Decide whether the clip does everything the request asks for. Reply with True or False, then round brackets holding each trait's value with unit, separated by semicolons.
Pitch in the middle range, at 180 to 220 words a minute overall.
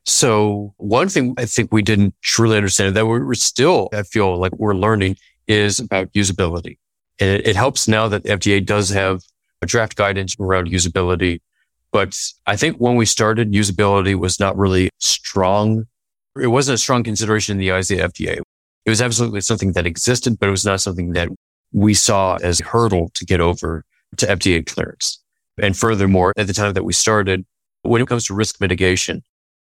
False (100 Hz; 190 wpm)